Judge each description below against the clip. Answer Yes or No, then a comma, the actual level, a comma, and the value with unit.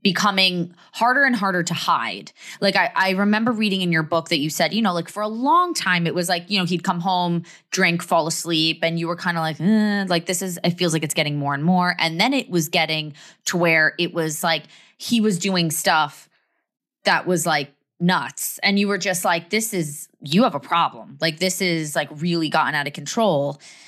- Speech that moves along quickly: Yes, fast, 230 wpm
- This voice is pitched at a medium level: Yes, medium, 175 Hz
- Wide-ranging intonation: No, average, 3.3 semitones